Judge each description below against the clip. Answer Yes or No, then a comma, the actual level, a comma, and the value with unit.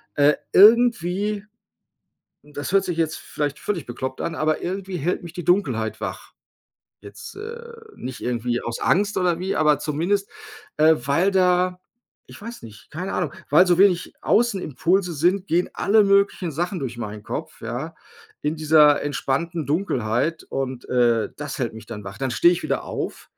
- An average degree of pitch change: No, wide, 5.8 semitones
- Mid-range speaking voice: Yes, medium, 160 Hz